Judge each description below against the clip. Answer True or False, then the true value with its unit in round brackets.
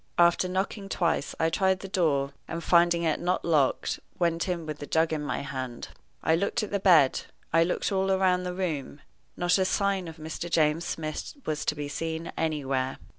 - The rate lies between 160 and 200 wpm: True (195 wpm)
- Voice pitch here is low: False (165 Hz)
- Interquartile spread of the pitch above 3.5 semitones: False (3.2 semitones)